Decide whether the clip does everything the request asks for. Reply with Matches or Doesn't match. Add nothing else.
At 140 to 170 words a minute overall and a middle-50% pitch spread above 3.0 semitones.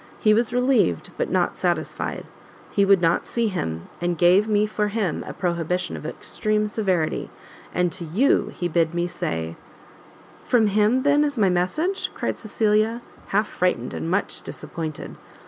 Matches